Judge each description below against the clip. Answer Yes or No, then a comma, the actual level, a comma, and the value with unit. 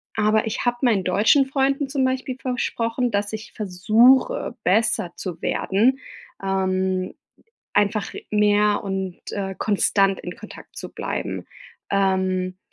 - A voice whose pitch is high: Yes, high, 210 Hz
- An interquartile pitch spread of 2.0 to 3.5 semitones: No, average, 4.0 semitones